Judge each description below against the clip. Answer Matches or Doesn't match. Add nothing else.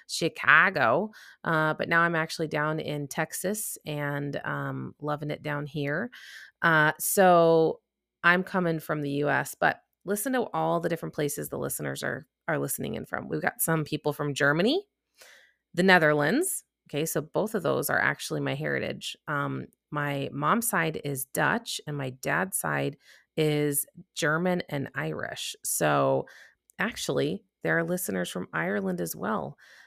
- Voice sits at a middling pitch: Matches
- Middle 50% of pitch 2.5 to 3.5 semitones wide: Matches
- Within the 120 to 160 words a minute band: Matches